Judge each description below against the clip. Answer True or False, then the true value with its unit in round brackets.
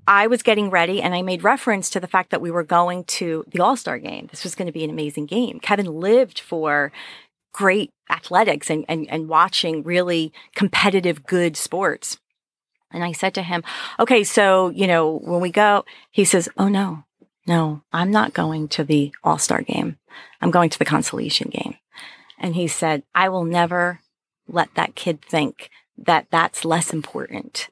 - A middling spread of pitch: True (3.6 semitones)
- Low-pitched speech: False (175 Hz)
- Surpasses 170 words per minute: True (185 wpm)